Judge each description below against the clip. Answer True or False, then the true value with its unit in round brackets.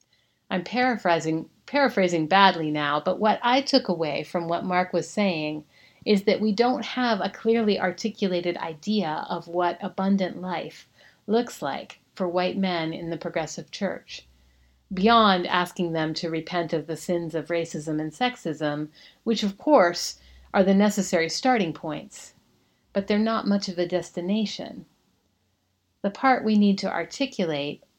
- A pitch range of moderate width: True (4.3 semitones)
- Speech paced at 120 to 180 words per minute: True (150 wpm)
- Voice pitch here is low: False (180 Hz)